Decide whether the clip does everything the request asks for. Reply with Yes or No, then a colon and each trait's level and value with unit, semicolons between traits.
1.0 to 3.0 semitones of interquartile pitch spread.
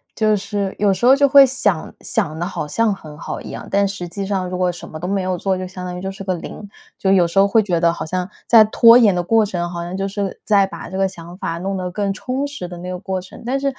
Yes: narrow, 2.4 semitones